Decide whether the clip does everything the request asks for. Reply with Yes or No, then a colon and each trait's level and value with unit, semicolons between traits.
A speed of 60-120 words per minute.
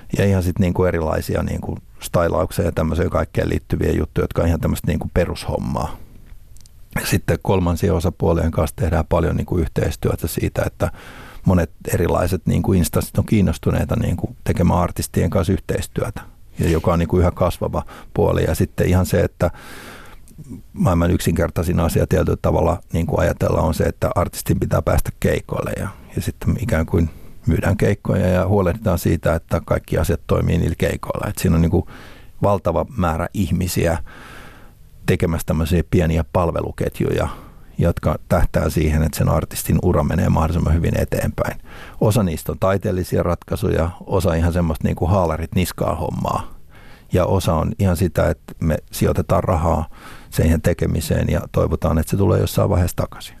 No: average, 150 wpm